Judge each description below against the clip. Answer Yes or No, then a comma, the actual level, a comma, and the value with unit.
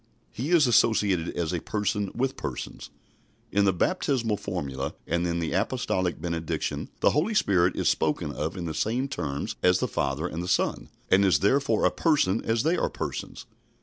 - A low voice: Yes, very low, 95 Hz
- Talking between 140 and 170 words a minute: No, average, 180 wpm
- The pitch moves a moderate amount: No, wide, 6.1 semitones